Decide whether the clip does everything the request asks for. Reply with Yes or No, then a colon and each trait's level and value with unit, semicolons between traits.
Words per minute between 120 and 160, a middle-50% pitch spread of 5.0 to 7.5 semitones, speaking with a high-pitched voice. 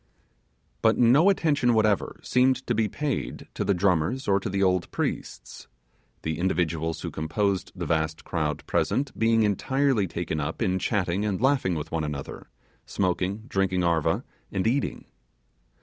No: average, 150 wpm; wide, 5.5 semitones; very low, 95 Hz